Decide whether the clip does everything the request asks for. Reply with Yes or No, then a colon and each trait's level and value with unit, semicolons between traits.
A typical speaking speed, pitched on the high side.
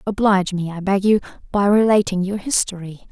Yes: average, 175 wpm; high, 195 Hz